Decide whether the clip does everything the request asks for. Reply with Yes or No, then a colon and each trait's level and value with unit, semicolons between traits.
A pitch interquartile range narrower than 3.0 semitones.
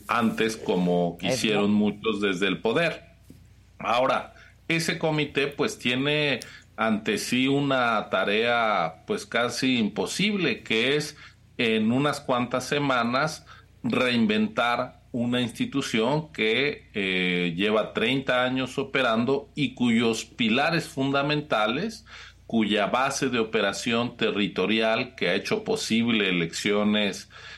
No: wide, 5.4 semitones